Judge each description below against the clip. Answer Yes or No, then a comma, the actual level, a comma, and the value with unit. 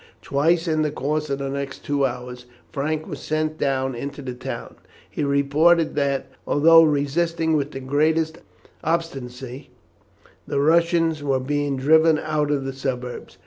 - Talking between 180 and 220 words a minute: No, average, 150 wpm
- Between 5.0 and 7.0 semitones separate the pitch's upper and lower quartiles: No, average, 2.7 semitones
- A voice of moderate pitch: Yes, medium, 145 Hz